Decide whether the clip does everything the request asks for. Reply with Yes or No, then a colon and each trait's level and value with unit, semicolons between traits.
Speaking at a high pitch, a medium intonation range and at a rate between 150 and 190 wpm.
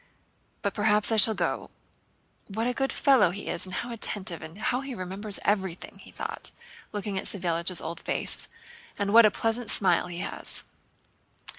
Yes: high, 205 Hz; average, 3.4 semitones; average, 170 wpm